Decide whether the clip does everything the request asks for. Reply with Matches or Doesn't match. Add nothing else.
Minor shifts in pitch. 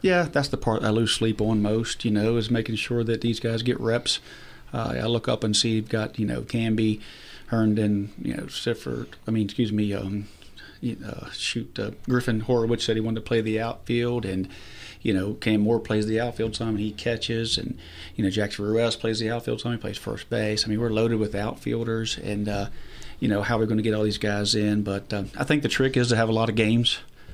Matches